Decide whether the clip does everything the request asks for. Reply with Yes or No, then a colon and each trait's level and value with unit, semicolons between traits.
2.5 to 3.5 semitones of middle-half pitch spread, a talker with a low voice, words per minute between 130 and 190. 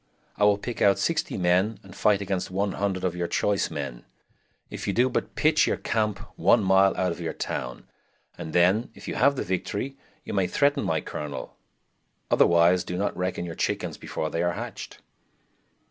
Yes: average, 2.9 semitones; very low, 95 Hz; average, 185 wpm